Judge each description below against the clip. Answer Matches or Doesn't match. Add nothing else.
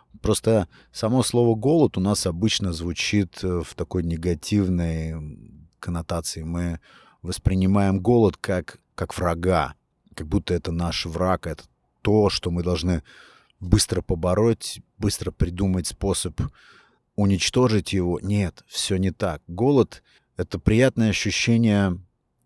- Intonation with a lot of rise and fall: Doesn't match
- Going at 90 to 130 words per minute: Matches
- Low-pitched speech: Matches